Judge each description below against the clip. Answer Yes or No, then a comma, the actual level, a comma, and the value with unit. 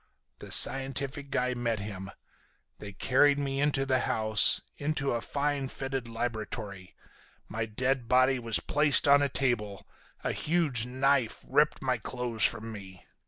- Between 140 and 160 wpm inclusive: Yes, average, 145 wpm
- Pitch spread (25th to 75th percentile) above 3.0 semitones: Yes, average, 3.6 semitones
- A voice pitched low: Yes, low, 125 Hz